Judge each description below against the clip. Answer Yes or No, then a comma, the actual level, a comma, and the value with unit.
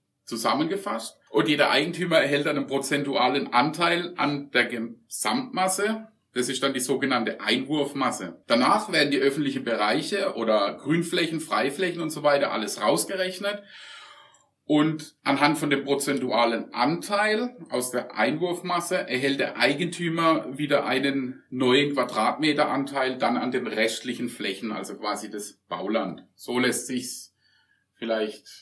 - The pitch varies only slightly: No, wide, 5.4 semitones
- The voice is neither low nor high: Yes, medium, 145 Hz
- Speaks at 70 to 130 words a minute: Yes, slow, 125 wpm